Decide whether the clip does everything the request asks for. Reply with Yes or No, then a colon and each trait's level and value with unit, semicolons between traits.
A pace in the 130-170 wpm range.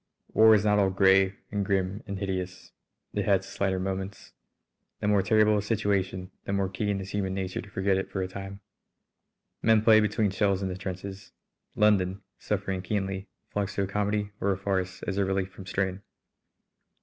No: average, 185 wpm